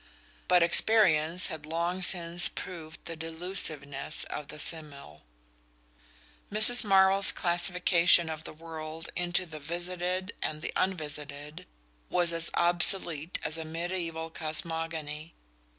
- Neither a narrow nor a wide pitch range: No, narrow, 2.3 semitones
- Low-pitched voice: No, medium, 165 Hz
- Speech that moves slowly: Yes, slow, 115 wpm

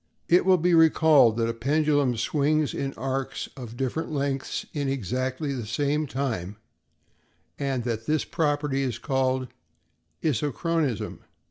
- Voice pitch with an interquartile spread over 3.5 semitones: No, average, 3.2 semitones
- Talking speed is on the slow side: Yes, slow, 130 wpm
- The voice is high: No, low, 135 Hz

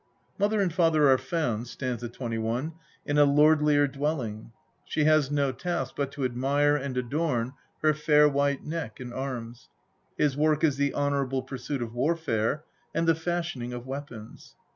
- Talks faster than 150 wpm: Yes, average, 160 wpm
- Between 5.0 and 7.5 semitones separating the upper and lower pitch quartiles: No, average, 3.5 semitones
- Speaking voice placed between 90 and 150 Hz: Yes, medium, 140 Hz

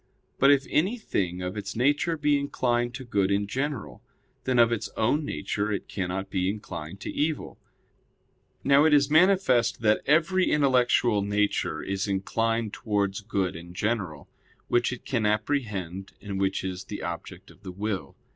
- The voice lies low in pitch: Yes, low, 110 Hz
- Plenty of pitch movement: Yes, wide, 5.8 semitones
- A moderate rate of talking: Yes, average, 160 wpm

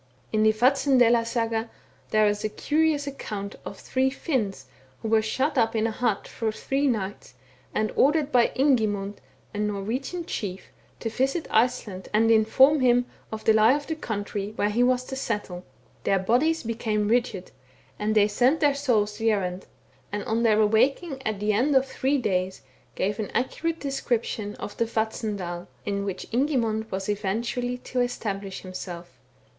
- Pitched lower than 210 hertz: No, high, 225 Hz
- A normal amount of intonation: Yes, average, 3.9 semitones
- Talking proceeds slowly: No, average, 165 wpm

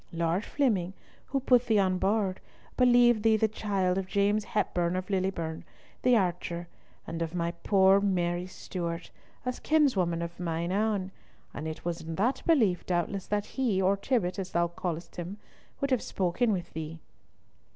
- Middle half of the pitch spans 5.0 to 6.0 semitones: No, average, 3.9 semitones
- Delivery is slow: No, average, 165 wpm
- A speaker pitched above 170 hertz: Yes, high, 190 Hz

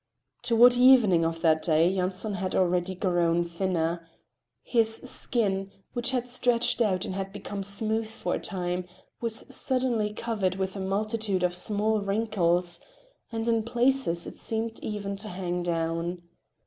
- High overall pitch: Yes, high, 195 Hz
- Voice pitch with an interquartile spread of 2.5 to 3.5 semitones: No, average, 4.0 semitones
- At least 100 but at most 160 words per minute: Yes, average, 150 wpm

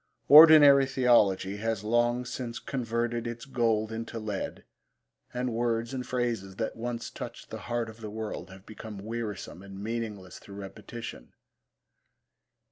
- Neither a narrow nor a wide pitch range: No, narrow, 2.3 semitones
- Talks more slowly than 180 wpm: Yes, slow, 135 wpm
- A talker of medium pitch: No, low, 115 Hz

